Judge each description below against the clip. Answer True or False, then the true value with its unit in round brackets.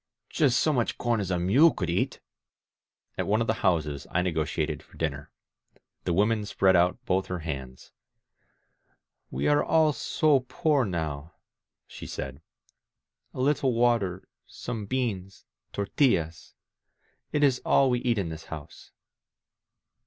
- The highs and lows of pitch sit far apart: True (7.2 semitones)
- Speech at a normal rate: True (155 wpm)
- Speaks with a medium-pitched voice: False (100 Hz)